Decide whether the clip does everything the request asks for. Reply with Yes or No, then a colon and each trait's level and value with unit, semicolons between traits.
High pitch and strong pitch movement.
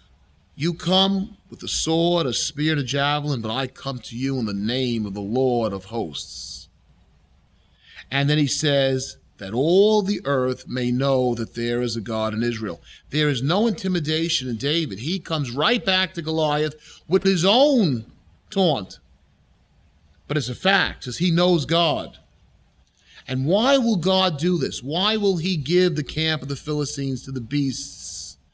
No: medium, 140 Hz; wide, 7.5 semitones